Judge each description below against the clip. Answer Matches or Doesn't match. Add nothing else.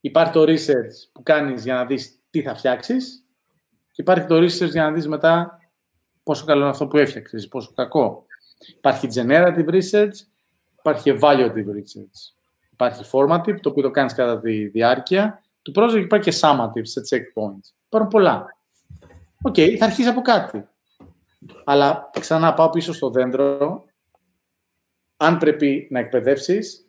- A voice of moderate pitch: Matches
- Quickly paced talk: Doesn't match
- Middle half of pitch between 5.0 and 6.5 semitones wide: Matches